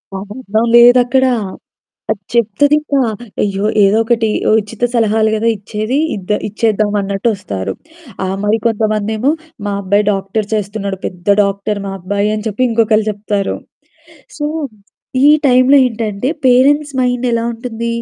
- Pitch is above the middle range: Yes, high, 215 Hz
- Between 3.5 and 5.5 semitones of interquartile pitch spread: No, average, 2.9 semitones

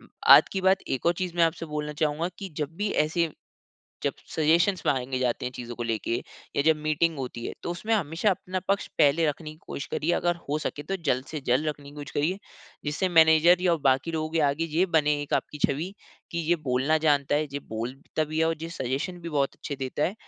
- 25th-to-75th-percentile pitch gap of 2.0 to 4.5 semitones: Yes, average, 3.2 semitones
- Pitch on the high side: No, medium, 155 Hz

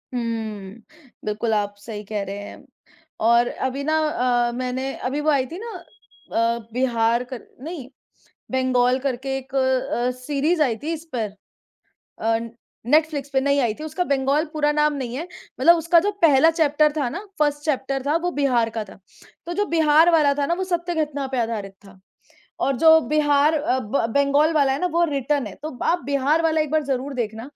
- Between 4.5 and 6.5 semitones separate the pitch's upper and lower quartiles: No, average, 3.9 semitones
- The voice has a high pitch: Yes, very high, 275 Hz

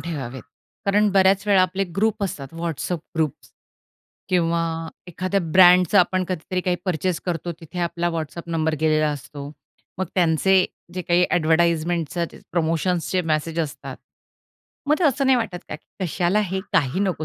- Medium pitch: Yes, medium, 175 Hz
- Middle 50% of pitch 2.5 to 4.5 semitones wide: Yes, average, 2.8 semitones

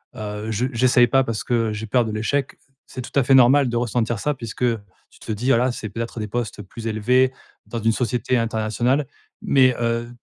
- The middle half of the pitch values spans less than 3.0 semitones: Yes, narrow, 2.4 semitones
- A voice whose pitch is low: Yes, low, 120 Hz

